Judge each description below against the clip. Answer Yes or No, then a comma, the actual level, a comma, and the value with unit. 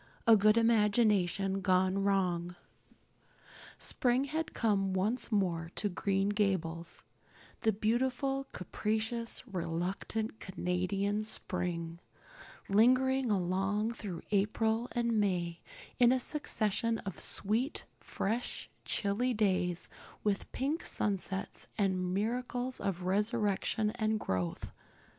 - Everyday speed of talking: No, slow, 100 wpm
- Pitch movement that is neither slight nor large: Yes, average, 3.6 semitones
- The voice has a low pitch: No, high, 205 Hz